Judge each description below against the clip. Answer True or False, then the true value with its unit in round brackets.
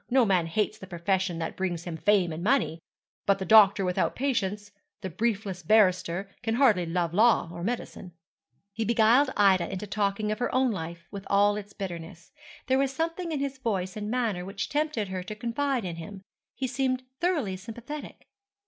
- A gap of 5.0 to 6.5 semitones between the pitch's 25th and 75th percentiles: False (4.6 semitones)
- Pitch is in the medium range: False (205 Hz)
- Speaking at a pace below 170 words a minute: False (185 wpm)